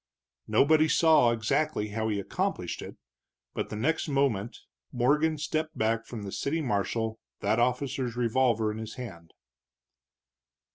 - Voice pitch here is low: Yes, low, 120 Hz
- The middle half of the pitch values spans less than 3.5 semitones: No, average, 4.4 semitones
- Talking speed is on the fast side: No, slow, 135 wpm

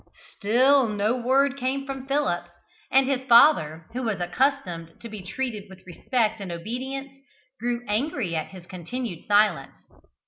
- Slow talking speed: No, average, 145 wpm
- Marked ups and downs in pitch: Yes, wide, 6.1 semitones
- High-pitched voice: Yes, high, 235 Hz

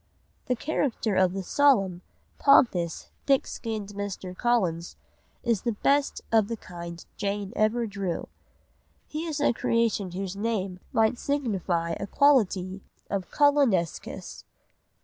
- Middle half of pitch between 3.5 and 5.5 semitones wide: Yes, average, 4.5 semitones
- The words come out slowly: Yes, slow, 130 wpm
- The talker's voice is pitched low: No, high, 205 Hz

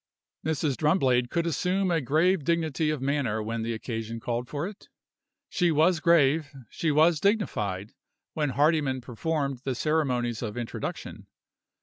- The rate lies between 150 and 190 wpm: No, average, 140 wpm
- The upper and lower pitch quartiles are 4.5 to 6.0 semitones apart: Yes, average, 5.0 semitones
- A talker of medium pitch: Yes, medium, 145 Hz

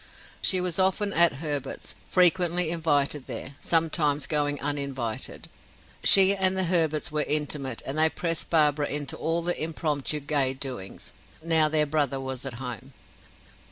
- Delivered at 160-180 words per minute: No, average, 150 wpm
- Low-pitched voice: No, medium, 150 Hz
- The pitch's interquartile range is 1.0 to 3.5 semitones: Yes, average, 3.2 semitones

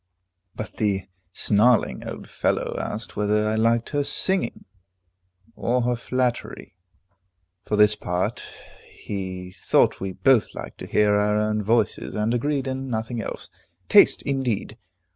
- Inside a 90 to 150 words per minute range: Yes, slow, 135 wpm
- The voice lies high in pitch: No, low, 110 Hz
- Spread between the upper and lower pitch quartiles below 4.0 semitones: Yes, average, 2.9 semitones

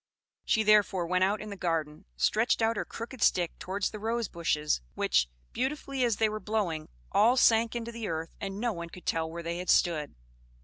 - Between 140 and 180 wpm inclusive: No, fast, 205 wpm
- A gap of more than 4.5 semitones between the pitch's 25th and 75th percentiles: Yes, average, 5.0 semitones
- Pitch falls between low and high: No, high, 200 Hz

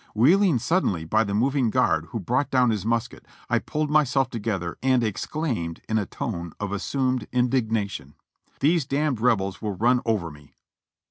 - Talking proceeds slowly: No, average, 160 wpm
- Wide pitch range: No, average, 4.8 semitones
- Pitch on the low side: Yes, low, 115 Hz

